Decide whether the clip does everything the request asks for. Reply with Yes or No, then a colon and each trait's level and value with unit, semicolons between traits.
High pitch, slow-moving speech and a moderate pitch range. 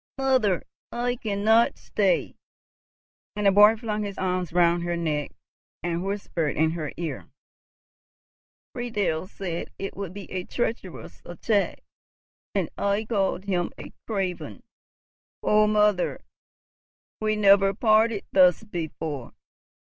Yes: high, 195 Hz; slow, 120 wpm; average, 3.6 semitones